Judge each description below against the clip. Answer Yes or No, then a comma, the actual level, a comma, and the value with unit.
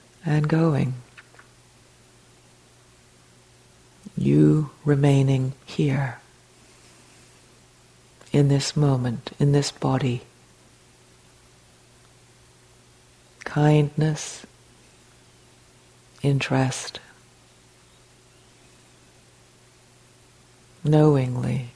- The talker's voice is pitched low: Yes, low, 130 Hz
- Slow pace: Yes, slow, 40 wpm